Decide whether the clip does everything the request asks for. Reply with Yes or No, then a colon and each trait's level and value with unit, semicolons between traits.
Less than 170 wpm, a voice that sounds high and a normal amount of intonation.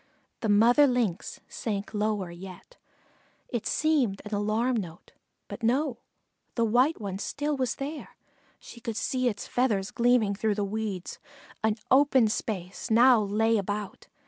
Yes: average, 145 wpm; high, 220 Hz; average, 3.6 semitones